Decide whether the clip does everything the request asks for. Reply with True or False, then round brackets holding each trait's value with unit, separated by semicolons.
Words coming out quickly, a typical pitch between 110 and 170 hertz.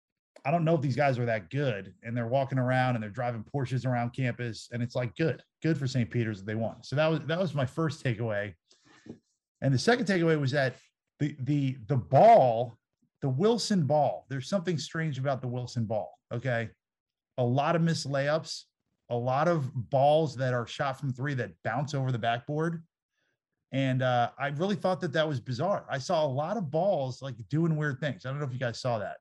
True (215 wpm; 135 Hz)